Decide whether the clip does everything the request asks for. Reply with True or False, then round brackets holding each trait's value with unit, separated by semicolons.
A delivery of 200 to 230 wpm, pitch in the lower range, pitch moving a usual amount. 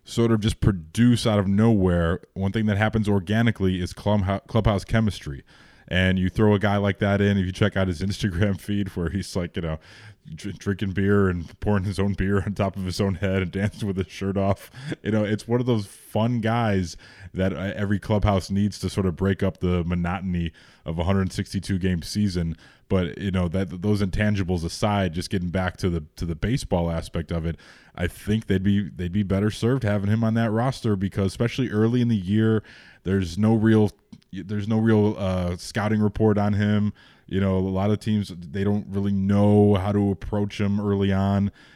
False (205 wpm; 100 Hz; 2.0 semitones)